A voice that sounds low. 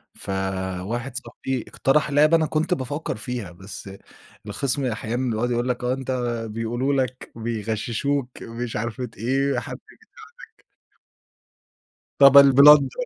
Yes: low, 125 Hz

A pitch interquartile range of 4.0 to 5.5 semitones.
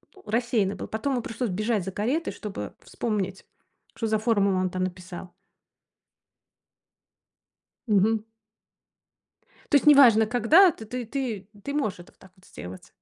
Yes: average, 4.3 semitones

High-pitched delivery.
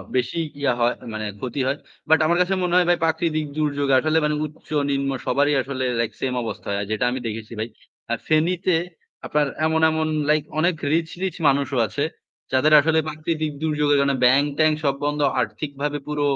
No: medium, 150 Hz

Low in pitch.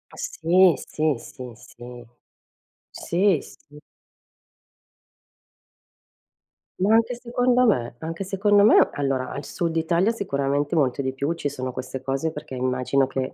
No: medium, 150 Hz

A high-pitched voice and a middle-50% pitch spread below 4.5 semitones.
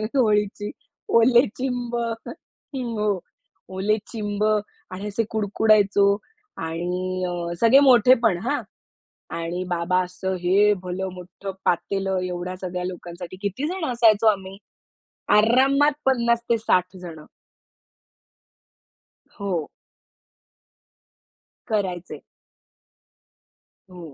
Yes: high, 200 Hz; average, 4.1 semitones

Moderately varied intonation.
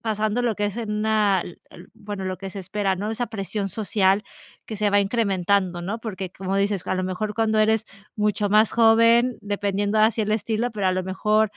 No: narrow, 2.1 semitones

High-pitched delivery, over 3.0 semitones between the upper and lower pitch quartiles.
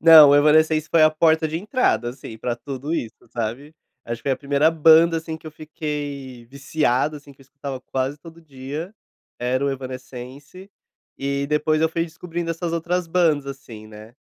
No: medium, 145 Hz; average, 3.4 semitones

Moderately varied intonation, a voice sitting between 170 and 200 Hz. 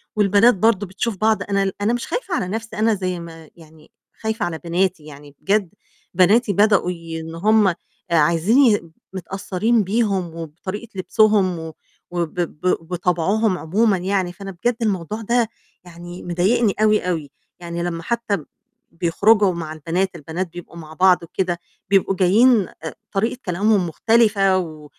Yes: average, 3.9 semitones; medium, 185 Hz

